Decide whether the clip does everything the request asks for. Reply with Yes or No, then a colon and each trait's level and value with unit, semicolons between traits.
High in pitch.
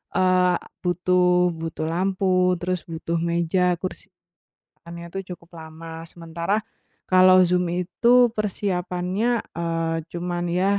No: medium, 180 Hz